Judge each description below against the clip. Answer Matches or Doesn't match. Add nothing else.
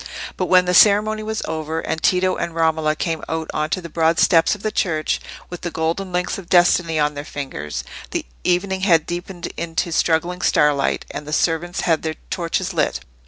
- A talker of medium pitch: Matches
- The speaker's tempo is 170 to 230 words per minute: Matches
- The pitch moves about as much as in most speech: Doesn't match